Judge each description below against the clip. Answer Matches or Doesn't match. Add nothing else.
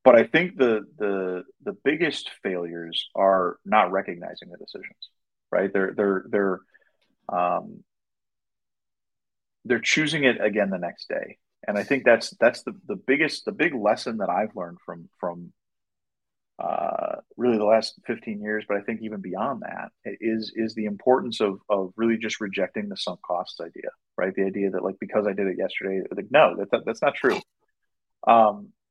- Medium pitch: Doesn't match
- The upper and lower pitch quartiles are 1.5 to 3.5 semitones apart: Matches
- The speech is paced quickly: Doesn't match